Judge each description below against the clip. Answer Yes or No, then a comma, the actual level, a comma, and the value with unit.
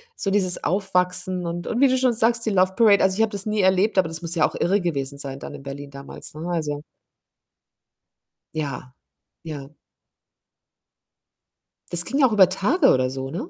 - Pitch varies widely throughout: Yes, wide, 5.8 semitones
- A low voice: No, medium, 180 Hz